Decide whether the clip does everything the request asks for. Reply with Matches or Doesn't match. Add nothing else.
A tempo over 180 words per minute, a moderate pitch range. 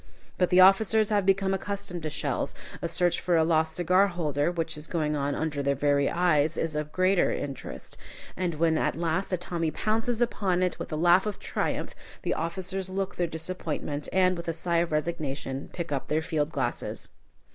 Matches